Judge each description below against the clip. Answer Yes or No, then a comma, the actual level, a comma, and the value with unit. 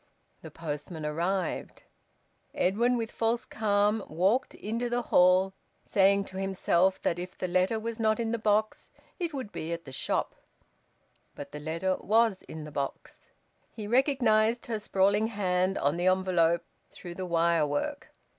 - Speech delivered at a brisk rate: No, average, 155 wpm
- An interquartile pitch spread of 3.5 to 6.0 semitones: Yes, average, 4.4 semitones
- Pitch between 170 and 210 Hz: Yes, high, 190 Hz